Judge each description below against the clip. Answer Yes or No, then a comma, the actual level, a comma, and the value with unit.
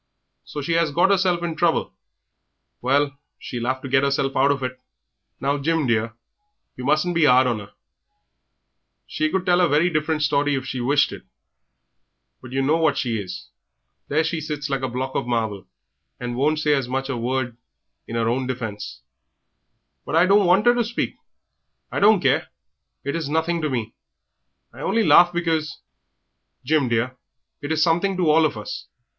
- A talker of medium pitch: Yes, medium, 145 Hz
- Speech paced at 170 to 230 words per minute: Yes, average, 185 wpm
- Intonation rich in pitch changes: No, average, 4.2 semitones